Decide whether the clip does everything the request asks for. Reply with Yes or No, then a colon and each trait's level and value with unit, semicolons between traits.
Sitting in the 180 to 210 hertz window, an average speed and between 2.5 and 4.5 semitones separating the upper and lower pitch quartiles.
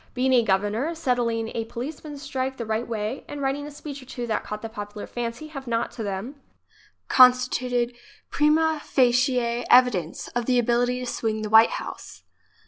No: high, 245 Hz; average, 175 wpm; average, 2.9 semitones